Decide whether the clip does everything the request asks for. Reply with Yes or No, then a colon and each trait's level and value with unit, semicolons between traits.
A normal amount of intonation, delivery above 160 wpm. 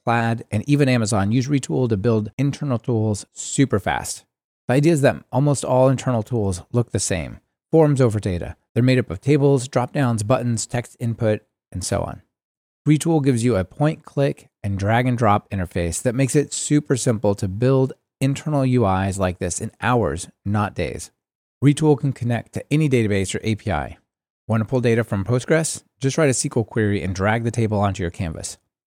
Yes: average, 4.7 semitones; average, 185 wpm